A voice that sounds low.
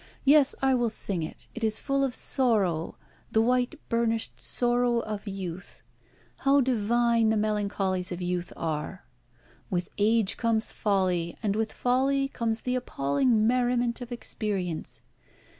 No: high, 225 Hz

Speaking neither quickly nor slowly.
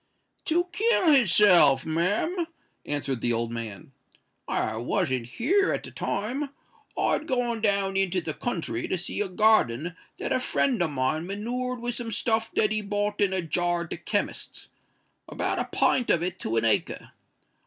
Yes: average, 170 wpm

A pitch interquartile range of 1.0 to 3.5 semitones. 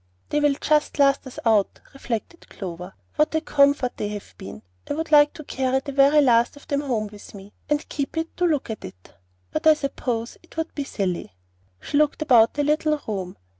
No: average, 5.2 semitones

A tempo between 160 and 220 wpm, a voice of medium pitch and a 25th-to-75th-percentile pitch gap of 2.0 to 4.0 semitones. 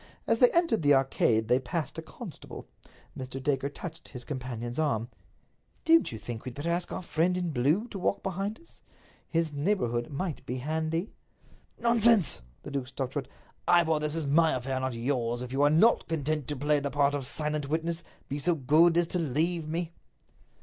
No: average, 190 wpm; medium, 150 Hz; average, 4.4 semitones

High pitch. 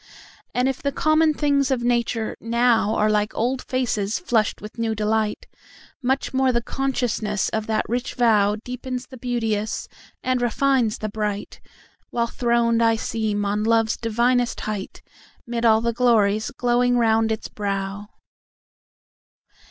Yes: high, 230 Hz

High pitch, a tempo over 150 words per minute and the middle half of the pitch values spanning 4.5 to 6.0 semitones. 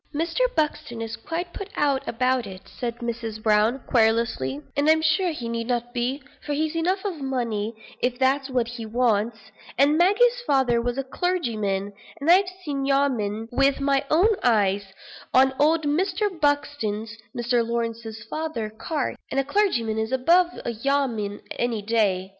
Yes: very high, 255 Hz; average, 160 wpm; average, 5.1 semitones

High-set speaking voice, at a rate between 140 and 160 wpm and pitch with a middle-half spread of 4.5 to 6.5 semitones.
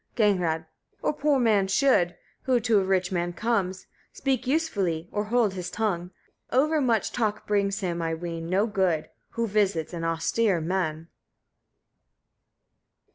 Yes: high, 195 Hz; average, 145 wpm; average, 4.8 semitones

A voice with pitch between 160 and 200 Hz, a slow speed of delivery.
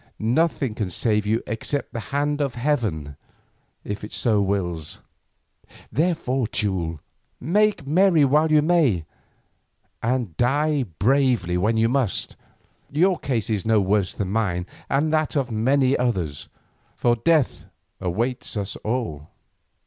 No: low, 120 Hz; slow, 125 wpm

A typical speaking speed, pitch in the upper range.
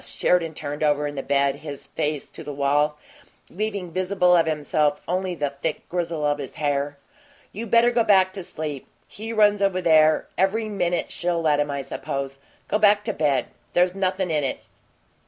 No: average, 185 wpm; medium, 165 Hz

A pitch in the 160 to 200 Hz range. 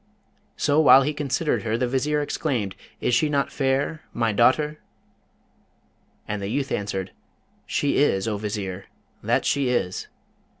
No: low, 130 Hz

